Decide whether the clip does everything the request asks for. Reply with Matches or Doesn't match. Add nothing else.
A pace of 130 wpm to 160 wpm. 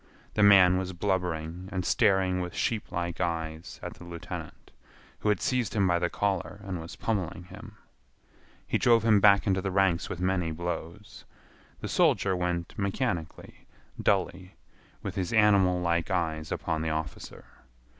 Matches